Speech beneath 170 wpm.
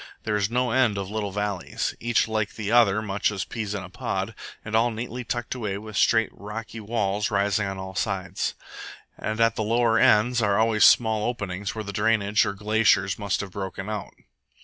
No: average, 195 wpm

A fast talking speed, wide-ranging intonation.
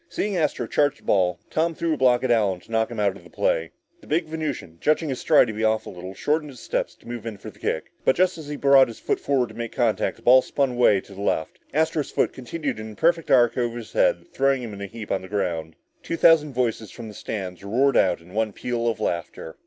Yes: fast, 260 wpm; wide, 6.0 semitones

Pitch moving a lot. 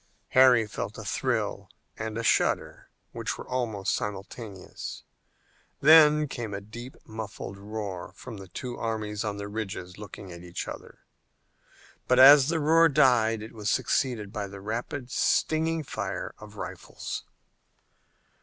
No: average, 4.1 semitones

